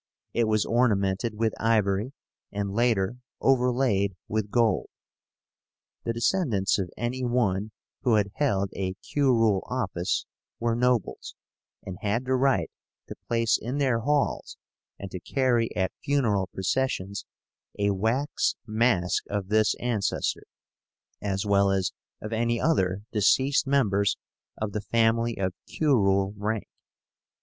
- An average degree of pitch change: Yes, average, 3.8 semitones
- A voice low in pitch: Yes, low, 110 Hz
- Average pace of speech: No, slow, 125 wpm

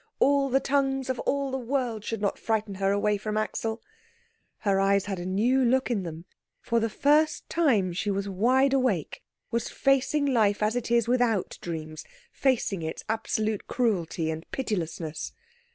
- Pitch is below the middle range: No, high, 220 Hz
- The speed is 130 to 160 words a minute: No, average, 170 wpm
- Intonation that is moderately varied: Yes, average, 4.9 semitones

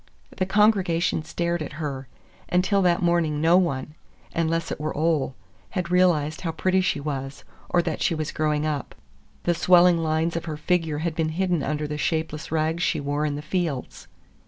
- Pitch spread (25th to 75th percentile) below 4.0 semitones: Yes, narrow, 2.5 semitones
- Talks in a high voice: No, medium, 160 Hz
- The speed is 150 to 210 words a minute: Yes, average, 175 wpm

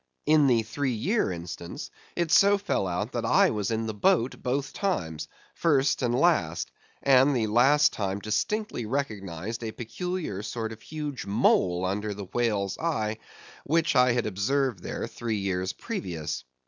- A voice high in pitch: No, low, 115 Hz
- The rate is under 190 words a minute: Yes, average, 160 wpm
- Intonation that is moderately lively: No, wide, 6.2 semitones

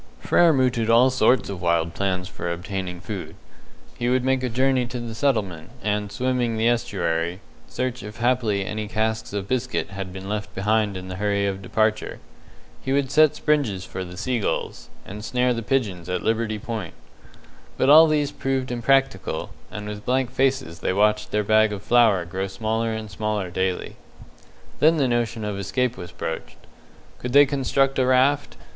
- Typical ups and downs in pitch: Yes, average, 4.7 semitones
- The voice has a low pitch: Yes, low, 110 Hz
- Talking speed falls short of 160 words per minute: No, average, 175 wpm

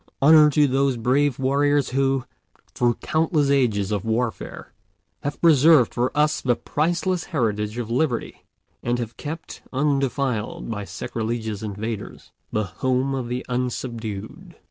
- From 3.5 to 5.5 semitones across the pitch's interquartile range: Yes, average, 4.0 semitones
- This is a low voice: Yes, low, 125 Hz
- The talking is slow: Yes, slow, 130 wpm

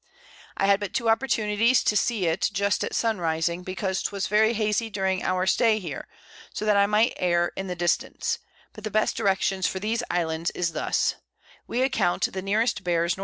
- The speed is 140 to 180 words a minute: No, average, 195 wpm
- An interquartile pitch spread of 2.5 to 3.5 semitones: Yes, average, 3.2 semitones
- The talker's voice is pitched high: Yes, high, 195 Hz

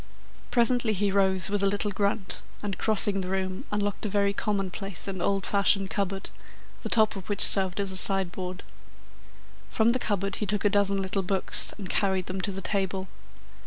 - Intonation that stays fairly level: Yes, narrow, 1.3 semitones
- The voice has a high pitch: Yes, high, 195 Hz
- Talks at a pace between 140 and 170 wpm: No, average, 185 wpm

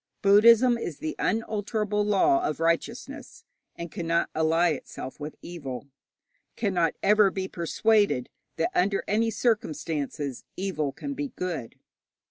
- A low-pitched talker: No, high, 190 Hz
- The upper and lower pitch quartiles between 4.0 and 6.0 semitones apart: Yes, average, 5.2 semitones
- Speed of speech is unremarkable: No, slow, 120 wpm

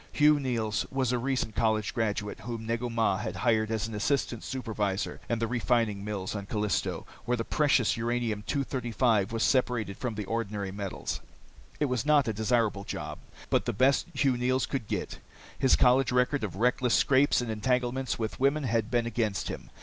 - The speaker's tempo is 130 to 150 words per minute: No, average, 180 wpm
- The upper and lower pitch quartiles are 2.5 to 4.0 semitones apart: Yes, average, 2.9 semitones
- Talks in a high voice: No, low, 115 Hz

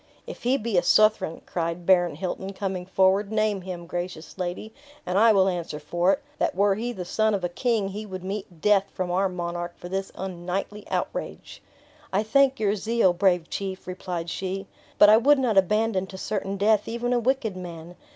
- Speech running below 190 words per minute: No, average, 195 wpm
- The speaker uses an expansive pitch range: No, average, 3.2 semitones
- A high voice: Yes, high, 195 Hz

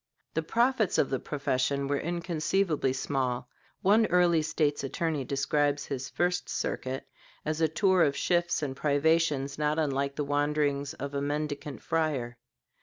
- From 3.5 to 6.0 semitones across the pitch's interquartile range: No, average, 2.9 semitones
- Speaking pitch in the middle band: Yes, medium, 145 Hz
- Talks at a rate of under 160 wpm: Yes, average, 145 wpm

